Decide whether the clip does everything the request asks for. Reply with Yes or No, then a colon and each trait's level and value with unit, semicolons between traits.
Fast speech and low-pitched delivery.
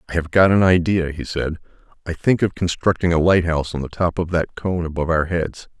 Yes: fast, 230 wpm; very low, 85 Hz